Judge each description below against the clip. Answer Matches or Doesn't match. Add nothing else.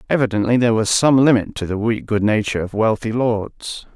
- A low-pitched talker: Matches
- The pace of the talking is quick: Doesn't match